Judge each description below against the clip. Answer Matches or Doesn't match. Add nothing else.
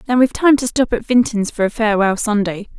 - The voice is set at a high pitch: Matches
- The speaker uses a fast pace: Matches